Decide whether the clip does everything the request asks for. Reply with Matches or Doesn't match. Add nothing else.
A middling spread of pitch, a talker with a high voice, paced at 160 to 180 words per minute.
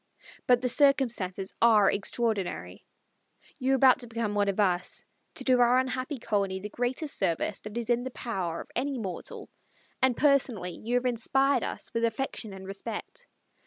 Matches